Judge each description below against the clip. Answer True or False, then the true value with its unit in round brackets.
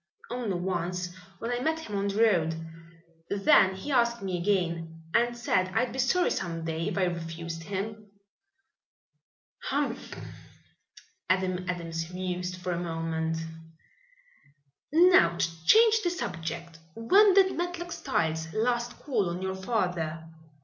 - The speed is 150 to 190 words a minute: False (135 wpm)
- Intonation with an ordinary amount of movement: False (6.0 semitones)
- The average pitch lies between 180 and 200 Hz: True (185 Hz)